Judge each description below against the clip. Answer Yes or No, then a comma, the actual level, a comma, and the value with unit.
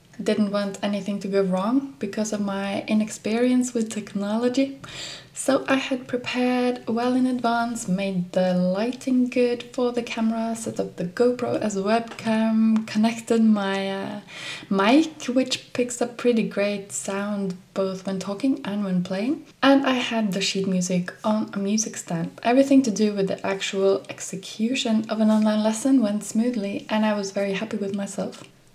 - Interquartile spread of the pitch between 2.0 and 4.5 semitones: Yes, average, 3.6 semitones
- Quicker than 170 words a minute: No, average, 165 wpm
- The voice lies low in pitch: No, high, 220 Hz